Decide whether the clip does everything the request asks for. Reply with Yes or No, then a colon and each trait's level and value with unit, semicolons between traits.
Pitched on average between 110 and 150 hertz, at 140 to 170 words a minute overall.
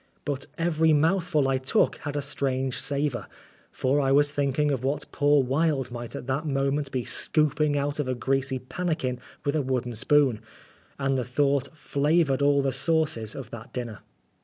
No: medium, 140 Hz; average, 180 wpm